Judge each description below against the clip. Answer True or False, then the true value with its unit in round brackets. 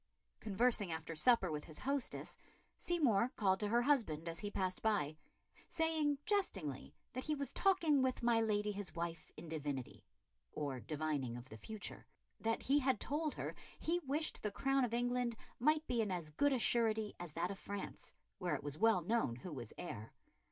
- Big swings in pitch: True (8.0 semitones)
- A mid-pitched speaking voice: False (215 Hz)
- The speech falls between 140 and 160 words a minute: False (185 wpm)